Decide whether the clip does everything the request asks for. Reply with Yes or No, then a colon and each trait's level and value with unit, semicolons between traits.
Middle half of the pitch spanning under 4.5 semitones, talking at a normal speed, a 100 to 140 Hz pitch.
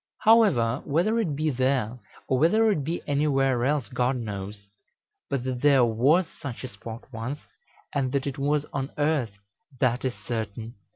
Yes: average, 3.8 semitones; average, 165 wpm; low, 135 Hz